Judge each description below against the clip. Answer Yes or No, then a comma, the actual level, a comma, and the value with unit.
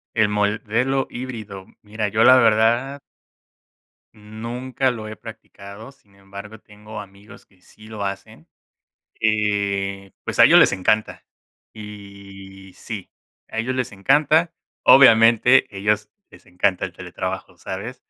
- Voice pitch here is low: Yes, low, 105 Hz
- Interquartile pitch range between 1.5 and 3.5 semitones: Yes, average, 2.8 semitones